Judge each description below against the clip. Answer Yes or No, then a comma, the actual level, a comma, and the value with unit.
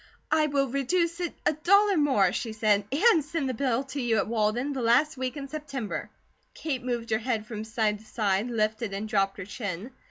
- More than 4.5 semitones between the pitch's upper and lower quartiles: Yes, average, 5.0 semitones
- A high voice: Yes, high, 245 Hz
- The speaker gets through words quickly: Yes, fast, 210 wpm